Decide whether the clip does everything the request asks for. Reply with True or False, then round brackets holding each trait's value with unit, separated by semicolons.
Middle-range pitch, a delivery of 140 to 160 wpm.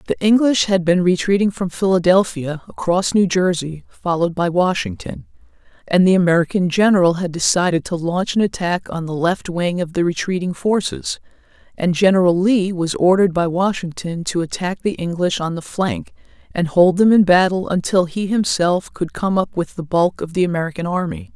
False (180 Hz; 175 wpm)